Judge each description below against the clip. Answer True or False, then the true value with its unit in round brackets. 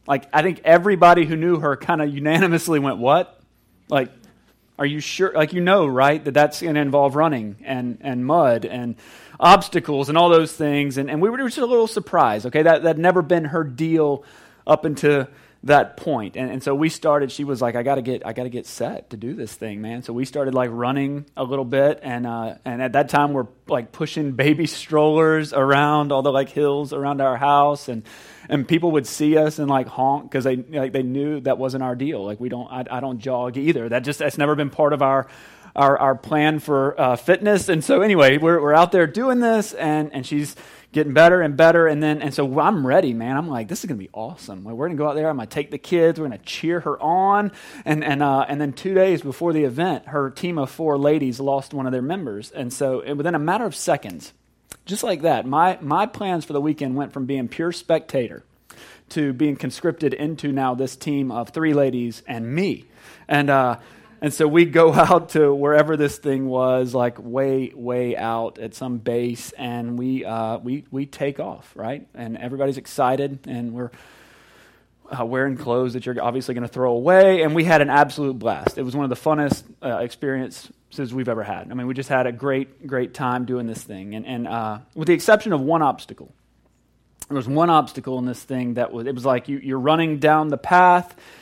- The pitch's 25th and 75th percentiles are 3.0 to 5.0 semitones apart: True (3.5 semitones)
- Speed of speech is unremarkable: False (225 wpm)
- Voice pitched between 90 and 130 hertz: False (140 Hz)